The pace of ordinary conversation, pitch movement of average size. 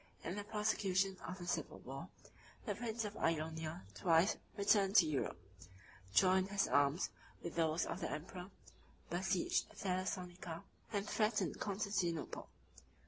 No: slow, 130 wpm; average, 3.3 semitones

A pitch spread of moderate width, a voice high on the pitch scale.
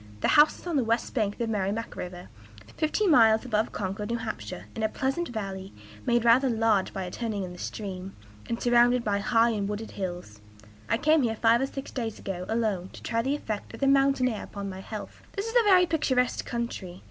Yes: average, 4.1 semitones; high, 225 Hz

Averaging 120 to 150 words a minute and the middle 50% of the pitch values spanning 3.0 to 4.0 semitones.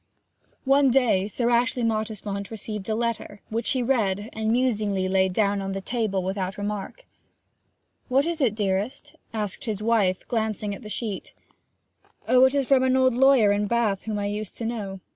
No: average, 180 wpm; average, 3.3 semitones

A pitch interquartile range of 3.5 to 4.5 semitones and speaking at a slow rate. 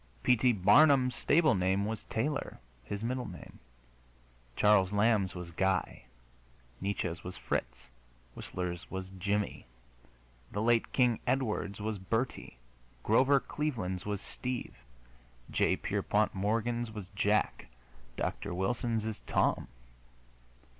Yes: average, 4.1 semitones; slow, 115 wpm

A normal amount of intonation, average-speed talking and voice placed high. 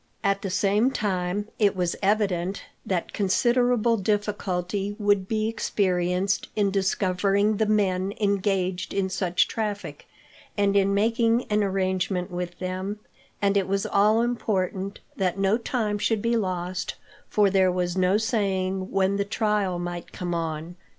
No: narrow, 2.2 semitones; average, 145 wpm; high, 195 Hz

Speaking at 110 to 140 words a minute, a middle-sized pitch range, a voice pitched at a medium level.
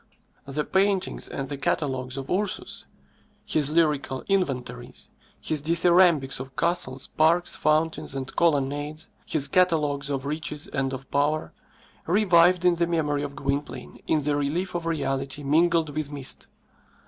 Yes: slow, 135 wpm; average, 3.4 semitones; medium, 150 Hz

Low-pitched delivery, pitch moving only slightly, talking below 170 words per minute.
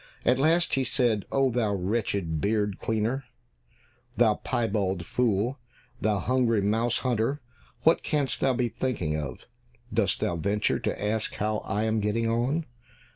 No: low, 110 Hz; average, 3.7 semitones; average, 145 wpm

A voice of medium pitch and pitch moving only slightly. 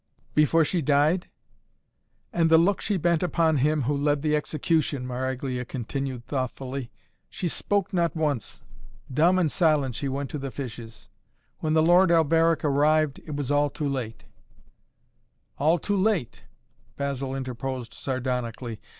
No: medium, 145 Hz; average, 3.8 semitones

